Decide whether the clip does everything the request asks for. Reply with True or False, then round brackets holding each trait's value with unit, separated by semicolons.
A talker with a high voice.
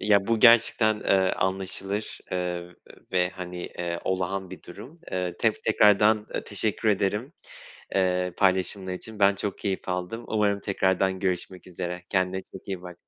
False (95 Hz)